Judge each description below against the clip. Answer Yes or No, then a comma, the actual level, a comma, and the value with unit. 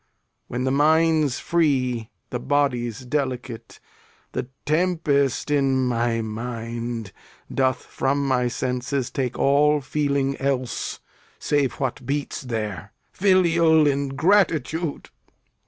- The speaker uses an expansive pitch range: No, average, 3.3 semitones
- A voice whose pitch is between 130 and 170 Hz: Yes, low, 135 Hz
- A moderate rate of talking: No, slow, 100 wpm